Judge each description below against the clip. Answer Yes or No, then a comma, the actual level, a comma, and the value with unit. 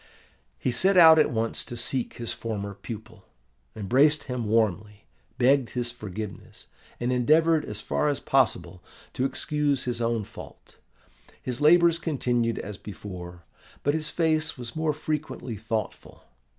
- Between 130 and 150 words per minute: Yes, average, 140 wpm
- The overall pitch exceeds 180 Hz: No, low, 120 Hz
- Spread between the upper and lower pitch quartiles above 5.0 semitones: Yes, wide, 5.4 semitones